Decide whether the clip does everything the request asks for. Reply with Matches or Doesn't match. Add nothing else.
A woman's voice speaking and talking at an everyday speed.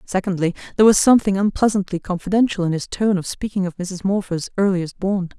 Matches